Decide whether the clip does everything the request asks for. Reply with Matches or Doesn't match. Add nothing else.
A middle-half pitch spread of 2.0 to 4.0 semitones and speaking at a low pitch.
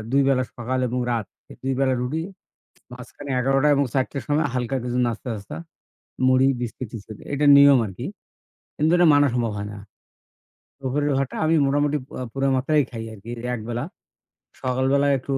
Matches